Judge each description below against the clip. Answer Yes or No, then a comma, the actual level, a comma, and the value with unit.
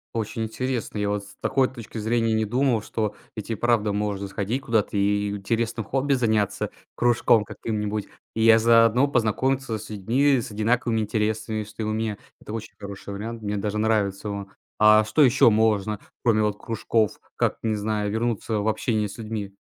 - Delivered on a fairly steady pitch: Yes, narrow, 1.9 semitones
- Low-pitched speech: Yes, low, 110 Hz